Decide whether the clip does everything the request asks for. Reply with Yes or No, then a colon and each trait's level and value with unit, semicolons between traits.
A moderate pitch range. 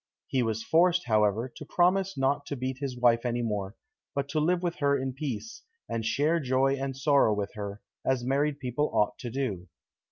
Yes: average, 4.0 semitones